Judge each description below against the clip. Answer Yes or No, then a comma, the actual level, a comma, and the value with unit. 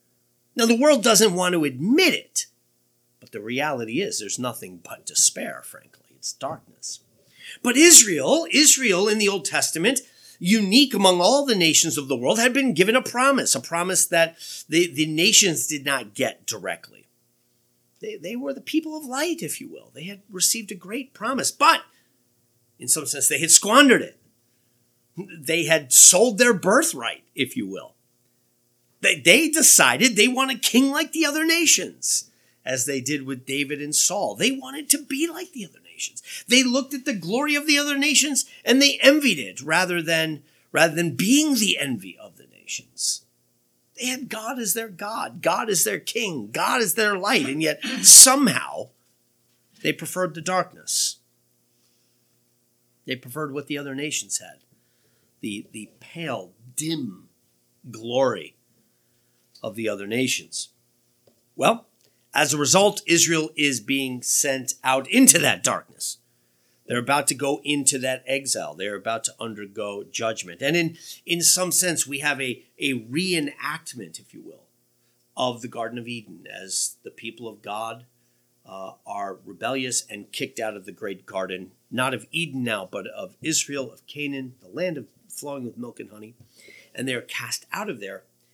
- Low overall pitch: No, medium, 150 Hz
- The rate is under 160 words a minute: No, average, 165 wpm